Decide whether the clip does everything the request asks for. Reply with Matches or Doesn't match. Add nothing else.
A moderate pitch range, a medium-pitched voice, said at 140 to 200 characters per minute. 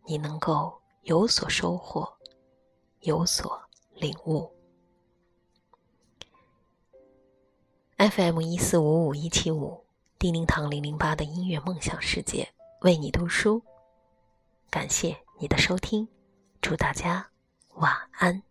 Matches